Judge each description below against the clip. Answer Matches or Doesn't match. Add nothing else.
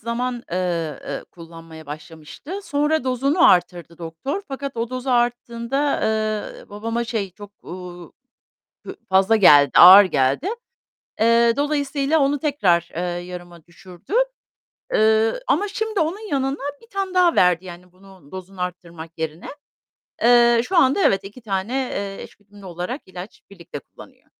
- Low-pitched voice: Doesn't match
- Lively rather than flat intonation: Matches